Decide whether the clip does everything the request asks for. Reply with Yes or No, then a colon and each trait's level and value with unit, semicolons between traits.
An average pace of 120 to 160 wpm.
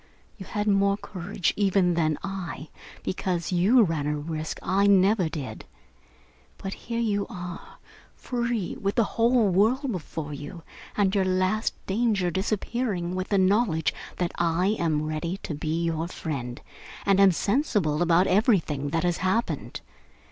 Yes: average, 150 wpm